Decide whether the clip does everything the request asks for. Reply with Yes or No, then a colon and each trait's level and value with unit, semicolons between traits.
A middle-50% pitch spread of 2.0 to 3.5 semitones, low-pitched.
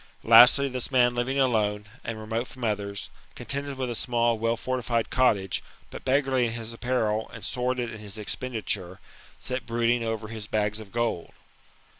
Yes: average, 2.7 semitones; low, 115 Hz